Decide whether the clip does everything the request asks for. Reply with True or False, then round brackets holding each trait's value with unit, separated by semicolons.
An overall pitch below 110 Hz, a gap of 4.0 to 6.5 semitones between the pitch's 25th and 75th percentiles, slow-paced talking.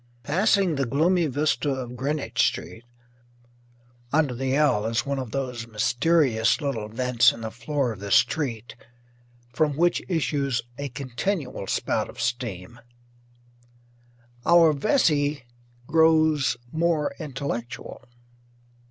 False (135 Hz; 4.4 semitones; 115 wpm)